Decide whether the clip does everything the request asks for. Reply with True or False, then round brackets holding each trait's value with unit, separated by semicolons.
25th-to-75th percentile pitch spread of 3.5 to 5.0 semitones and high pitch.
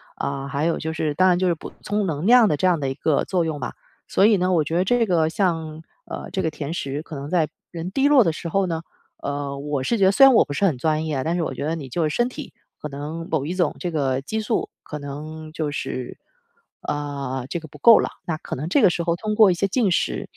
False (4.3 semitones; 160 Hz)